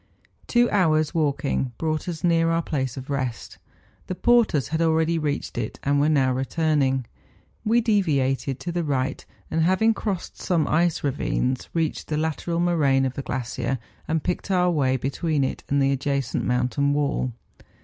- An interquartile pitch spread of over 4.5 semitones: No, average, 3.9 semitones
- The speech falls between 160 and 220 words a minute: Yes, average, 165 wpm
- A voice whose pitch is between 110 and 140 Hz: No, medium, 150 Hz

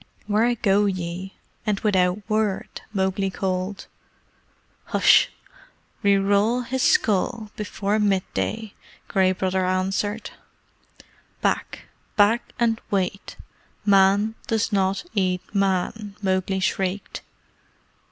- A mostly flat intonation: Yes, narrow, 2.0 semitones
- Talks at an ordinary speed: No, slow, 105 wpm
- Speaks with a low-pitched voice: No, high, 200 Hz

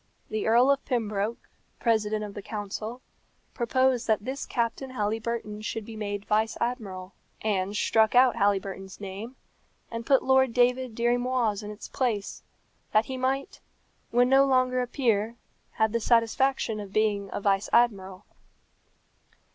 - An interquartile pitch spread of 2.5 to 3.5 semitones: Yes, average, 3.2 semitones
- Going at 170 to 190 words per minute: No, average, 145 wpm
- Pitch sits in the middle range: No, high, 225 Hz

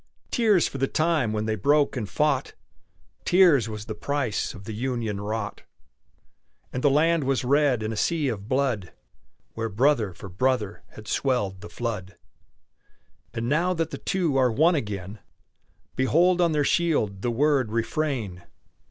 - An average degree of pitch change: No, wide, 5.7 semitones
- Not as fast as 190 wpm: Yes, average, 160 wpm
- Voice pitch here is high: No, low, 125 Hz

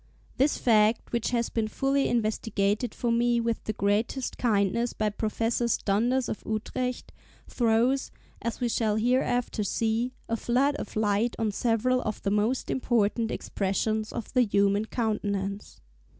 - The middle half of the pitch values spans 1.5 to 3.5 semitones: Yes, narrow, 2.4 semitones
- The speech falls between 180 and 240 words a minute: No, average, 145 wpm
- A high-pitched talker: Yes, high, 225 Hz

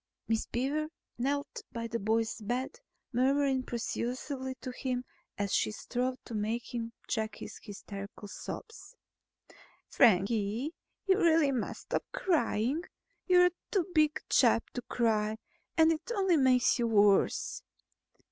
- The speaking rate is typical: No, slow, 130 wpm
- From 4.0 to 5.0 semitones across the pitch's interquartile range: Yes, average, 4.6 semitones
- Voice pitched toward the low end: No, very high, 250 Hz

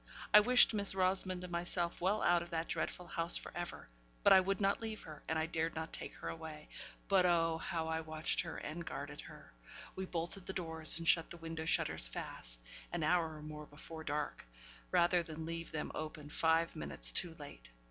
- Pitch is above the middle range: No, medium, 165 Hz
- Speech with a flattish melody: Yes, narrow, 2.0 semitones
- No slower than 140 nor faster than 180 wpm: No, fast, 205 wpm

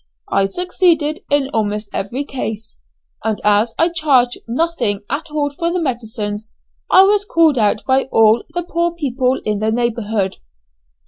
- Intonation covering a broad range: Yes, wide, 6.8 semitones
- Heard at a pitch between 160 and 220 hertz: No, very high, 255 Hz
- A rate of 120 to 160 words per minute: Yes, average, 150 wpm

